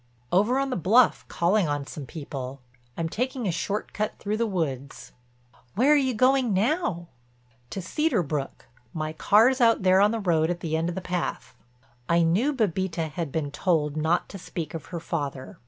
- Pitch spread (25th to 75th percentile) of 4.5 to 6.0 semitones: Yes, wide, 5.6 semitones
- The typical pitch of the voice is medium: Yes, medium, 180 Hz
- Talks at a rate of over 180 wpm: Yes, average, 190 wpm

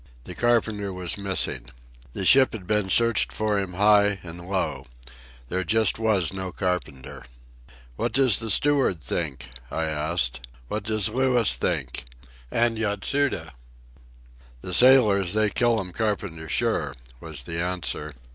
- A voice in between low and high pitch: No, very low, 95 Hz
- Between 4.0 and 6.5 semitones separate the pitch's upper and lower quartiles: Yes, average, 4.7 semitones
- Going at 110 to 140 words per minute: Yes, slow, 135 wpm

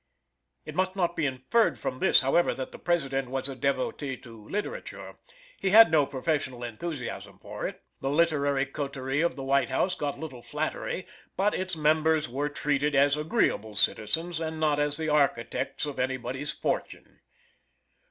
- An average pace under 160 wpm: No, average, 165 wpm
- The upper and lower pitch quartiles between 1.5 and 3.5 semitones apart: Yes, average, 3.2 semitones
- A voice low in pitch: No, medium, 145 Hz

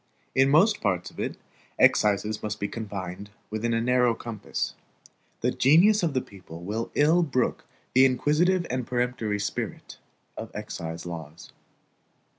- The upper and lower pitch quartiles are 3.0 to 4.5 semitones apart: No, average, 4.9 semitones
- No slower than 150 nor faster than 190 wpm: No, average, 140 wpm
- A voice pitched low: Yes, low, 115 Hz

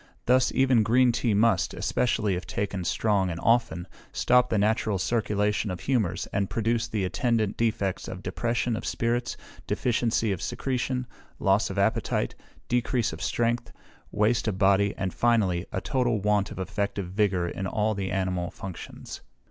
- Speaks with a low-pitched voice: Yes, low, 105 Hz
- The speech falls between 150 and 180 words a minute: Yes, average, 155 wpm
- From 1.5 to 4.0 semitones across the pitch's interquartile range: Yes, average, 3.5 semitones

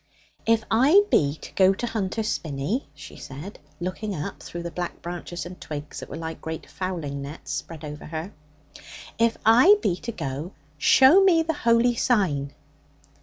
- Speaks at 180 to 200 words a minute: No, average, 170 wpm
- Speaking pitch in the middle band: Yes, medium, 180 Hz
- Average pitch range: No, wide, 6.8 semitones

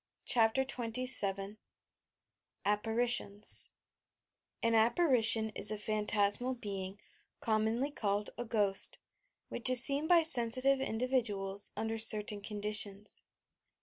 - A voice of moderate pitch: No, high, 220 Hz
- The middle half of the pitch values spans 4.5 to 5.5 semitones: No, average, 3.1 semitones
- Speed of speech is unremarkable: No, slow, 100 wpm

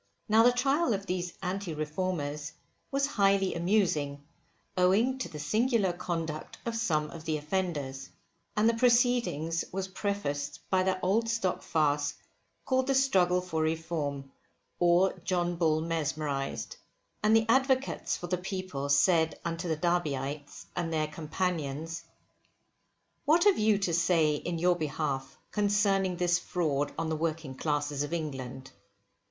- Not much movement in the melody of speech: No, average, 4.5 semitones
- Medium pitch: Yes, medium, 175 Hz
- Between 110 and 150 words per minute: Yes, average, 140 wpm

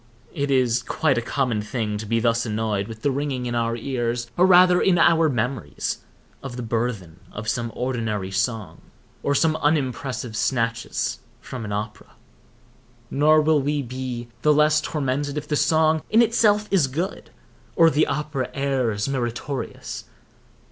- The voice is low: Yes, low, 130 Hz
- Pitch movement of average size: Yes, average, 4.5 semitones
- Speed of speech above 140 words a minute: Yes, average, 155 wpm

